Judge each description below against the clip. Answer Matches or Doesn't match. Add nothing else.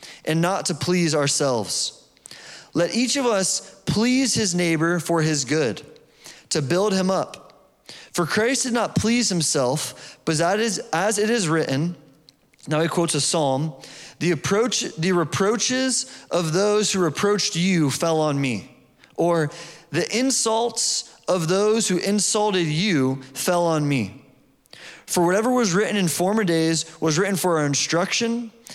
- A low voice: Doesn't match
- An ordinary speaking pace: Matches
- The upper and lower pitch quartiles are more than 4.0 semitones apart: Matches